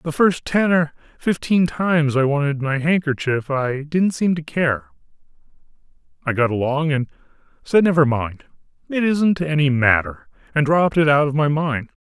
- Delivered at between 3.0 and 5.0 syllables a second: Yes, 4.7 syllables/s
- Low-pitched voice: No, medium, 150 Hz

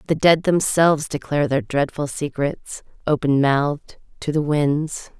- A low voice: No, medium, 145 Hz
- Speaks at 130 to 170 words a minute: Yes, average, 140 wpm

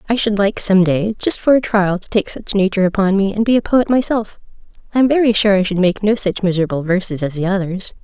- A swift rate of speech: Yes, fast, 255 wpm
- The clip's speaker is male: No, female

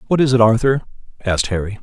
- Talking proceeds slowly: No, average, 200 wpm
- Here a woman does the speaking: No, male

